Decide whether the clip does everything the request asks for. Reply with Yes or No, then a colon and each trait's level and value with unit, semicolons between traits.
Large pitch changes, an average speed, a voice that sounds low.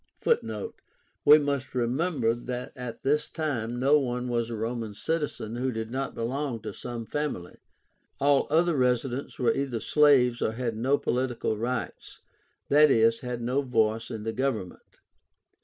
No: average, 3.4 semitones; average, 150 wpm; low, 125 Hz